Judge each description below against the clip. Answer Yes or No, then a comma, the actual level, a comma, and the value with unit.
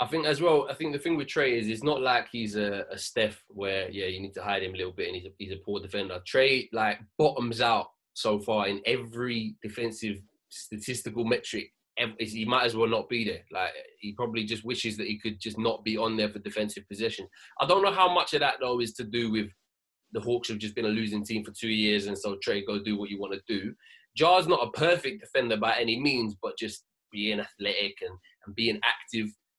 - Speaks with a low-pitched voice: Yes, low, 110 Hz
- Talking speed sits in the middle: No, fast, 240 wpm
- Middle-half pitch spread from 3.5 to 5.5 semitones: No, average, 2.7 semitones